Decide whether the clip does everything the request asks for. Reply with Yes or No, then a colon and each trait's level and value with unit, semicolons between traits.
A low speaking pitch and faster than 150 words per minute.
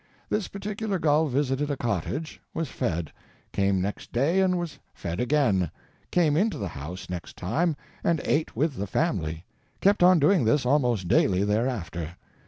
Yes: low, 130 Hz; average, 160 wpm